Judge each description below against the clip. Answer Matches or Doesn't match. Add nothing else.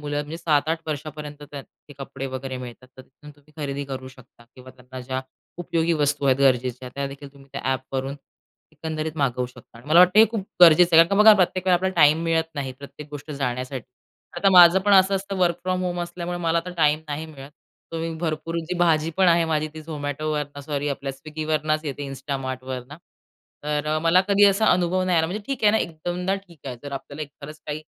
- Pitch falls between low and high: Matches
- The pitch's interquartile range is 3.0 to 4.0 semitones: Matches